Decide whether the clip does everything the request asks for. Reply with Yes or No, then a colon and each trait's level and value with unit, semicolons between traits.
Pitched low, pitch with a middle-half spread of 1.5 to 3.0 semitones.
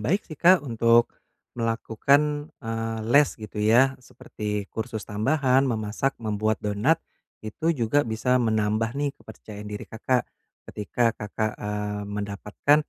No: low, 115 Hz; average, 3.7 semitones